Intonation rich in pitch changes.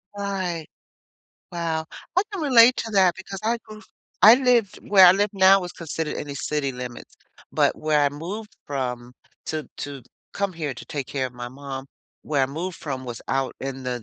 Yes: wide, 6.5 semitones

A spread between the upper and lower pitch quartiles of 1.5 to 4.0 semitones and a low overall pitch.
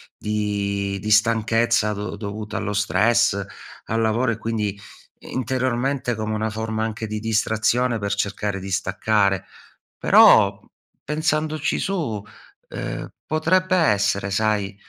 Yes: narrow, 2.5 semitones; low, 110 Hz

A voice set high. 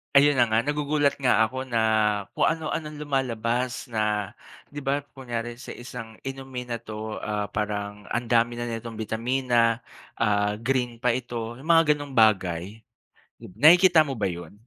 No: low, 120 Hz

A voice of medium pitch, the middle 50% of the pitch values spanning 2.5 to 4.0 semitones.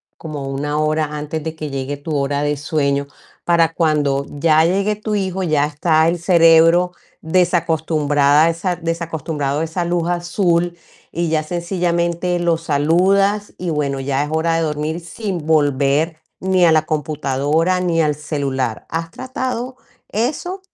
Yes: medium, 160 Hz; average, 2.9 semitones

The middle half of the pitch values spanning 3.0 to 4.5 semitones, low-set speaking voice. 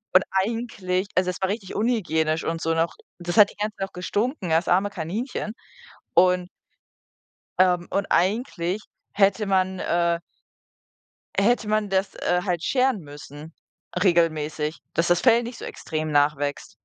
No: average, 3.7 semitones; medium, 185 Hz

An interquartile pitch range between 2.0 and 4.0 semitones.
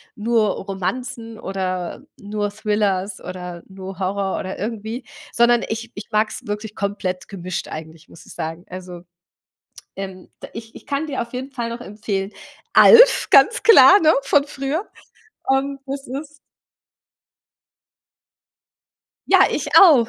No: average, 5.0 semitones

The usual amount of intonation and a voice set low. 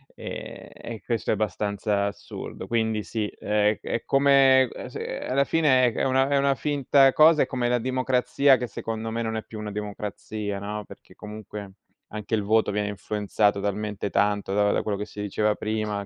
Yes: average, 3.6 semitones; low, 110 Hz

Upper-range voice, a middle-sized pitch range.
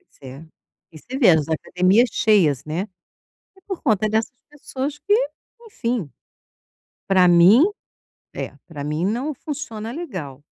No: high, 215 Hz; wide, 8.1 semitones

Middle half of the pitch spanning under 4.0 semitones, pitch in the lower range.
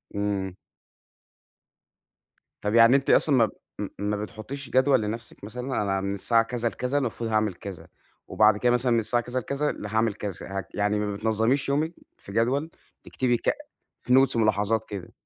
Yes: average, 3.3 semitones; low, 115 Hz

